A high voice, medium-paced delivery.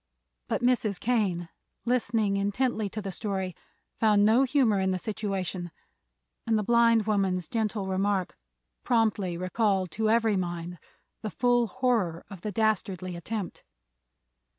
No: high, 205 Hz; slow, 130 wpm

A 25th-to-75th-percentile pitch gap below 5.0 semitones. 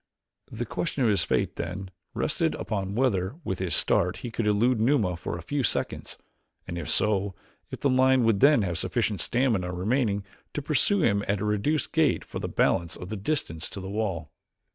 No: average, 5.3 semitones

